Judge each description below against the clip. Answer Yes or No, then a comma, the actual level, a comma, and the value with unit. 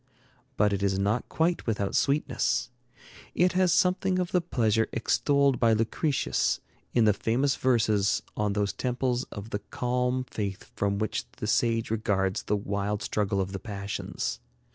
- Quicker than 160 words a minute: No, average, 155 wpm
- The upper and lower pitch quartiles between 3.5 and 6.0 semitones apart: Yes, average, 4.1 semitones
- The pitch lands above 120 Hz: No, low, 110 Hz